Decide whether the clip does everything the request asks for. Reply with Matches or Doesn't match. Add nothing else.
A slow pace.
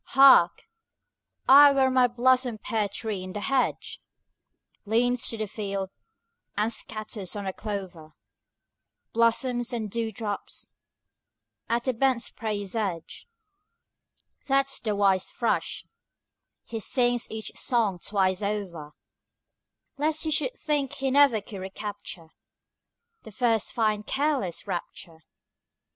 Matches